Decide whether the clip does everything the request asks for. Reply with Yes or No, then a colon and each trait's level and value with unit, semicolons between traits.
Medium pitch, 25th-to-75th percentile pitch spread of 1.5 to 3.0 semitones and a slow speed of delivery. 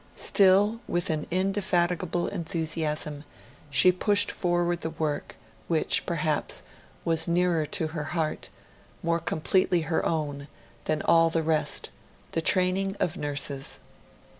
Yes: medium, 165 Hz; narrow, 2.6 semitones; slow, 120 wpm